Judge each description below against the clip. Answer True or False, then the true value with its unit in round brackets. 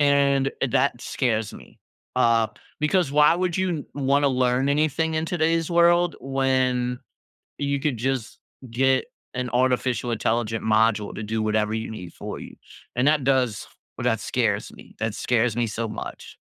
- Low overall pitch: True (130 Hz)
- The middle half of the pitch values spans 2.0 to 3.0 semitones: False (4.0 semitones)